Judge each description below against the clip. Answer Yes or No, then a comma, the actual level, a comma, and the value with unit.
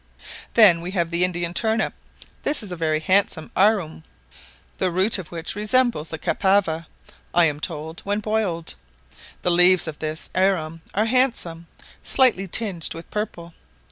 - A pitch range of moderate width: Yes, average, 3.9 semitones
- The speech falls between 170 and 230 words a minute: No, average, 150 wpm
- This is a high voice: No, medium, 180 Hz